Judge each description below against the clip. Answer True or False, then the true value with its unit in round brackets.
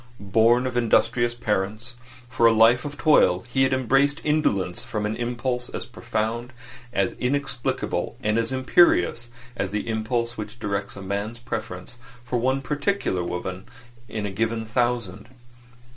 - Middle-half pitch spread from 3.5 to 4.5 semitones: False (2.9 semitones)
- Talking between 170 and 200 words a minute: False (145 wpm)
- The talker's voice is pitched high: False (115 Hz)